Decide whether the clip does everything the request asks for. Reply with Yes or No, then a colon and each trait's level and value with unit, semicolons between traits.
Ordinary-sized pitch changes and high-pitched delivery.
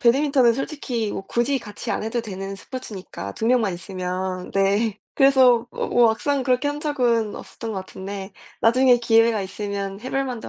Yes: average, 4.4 semitones; high, 230 Hz